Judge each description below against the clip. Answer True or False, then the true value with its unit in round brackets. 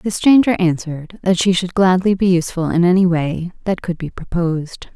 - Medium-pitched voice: True (180 Hz)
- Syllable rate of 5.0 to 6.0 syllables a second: True (5.3 syllables/s)